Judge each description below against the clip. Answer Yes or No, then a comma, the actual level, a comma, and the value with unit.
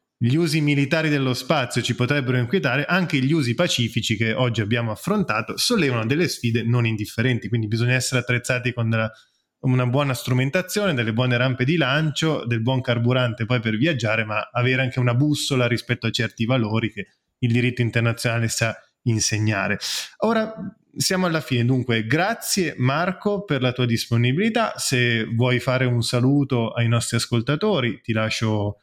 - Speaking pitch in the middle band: No, low, 125 Hz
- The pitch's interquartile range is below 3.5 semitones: No, average, 3.8 semitones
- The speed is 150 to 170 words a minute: Yes, average, 160 wpm